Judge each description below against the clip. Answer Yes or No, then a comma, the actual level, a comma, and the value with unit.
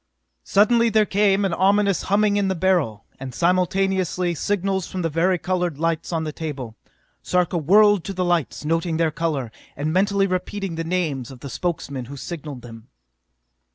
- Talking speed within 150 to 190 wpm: Yes, average, 170 wpm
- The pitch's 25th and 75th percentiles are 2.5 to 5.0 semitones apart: Yes, average, 3.9 semitones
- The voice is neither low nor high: Yes, medium, 175 Hz